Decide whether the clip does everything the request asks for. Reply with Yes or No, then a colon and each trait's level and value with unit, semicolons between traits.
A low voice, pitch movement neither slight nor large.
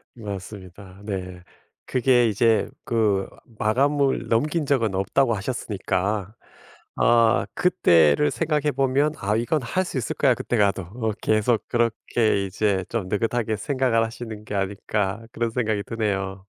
Yes: low, 110 Hz; average, 3.6 semitones